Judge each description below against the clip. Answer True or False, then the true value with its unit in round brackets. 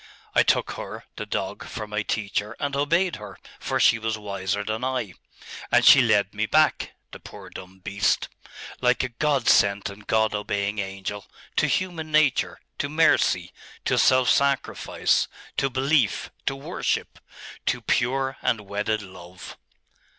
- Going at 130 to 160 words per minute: True (150 wpm)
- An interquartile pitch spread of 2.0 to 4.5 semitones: False (5.0 semitones)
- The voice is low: True (110 Hz)